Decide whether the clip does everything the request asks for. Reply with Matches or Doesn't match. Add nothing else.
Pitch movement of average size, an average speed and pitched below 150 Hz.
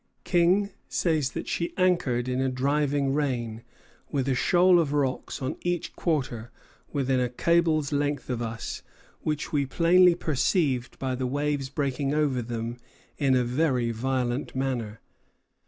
Matches